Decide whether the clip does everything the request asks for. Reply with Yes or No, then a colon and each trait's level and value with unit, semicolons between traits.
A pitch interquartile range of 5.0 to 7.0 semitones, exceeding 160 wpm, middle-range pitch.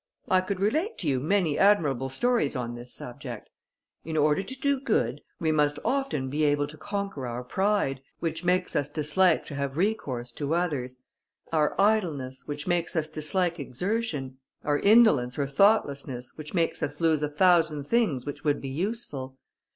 Yes: wide, 5.6 semitones; average, 170 wpm; medium, 155 Hz